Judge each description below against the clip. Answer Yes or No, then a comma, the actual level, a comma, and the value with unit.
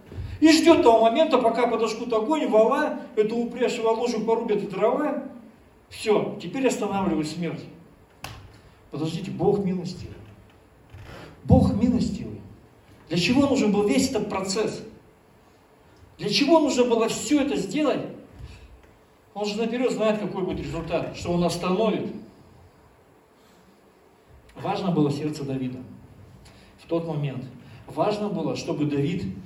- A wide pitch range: Yes, wide, 6.9 semitones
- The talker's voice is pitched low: No, high, 200 Hz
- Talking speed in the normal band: Yes, average, 120 wpm